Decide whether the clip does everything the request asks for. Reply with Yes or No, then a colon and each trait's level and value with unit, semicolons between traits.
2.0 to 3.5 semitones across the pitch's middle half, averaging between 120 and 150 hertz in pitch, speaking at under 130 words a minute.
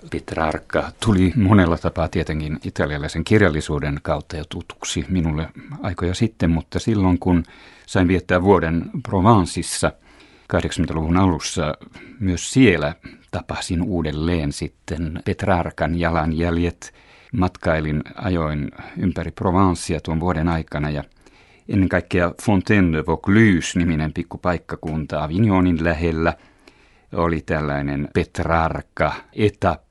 No: narrow, 2.6 semitones; very low, 85 Hz; average, 100 wpm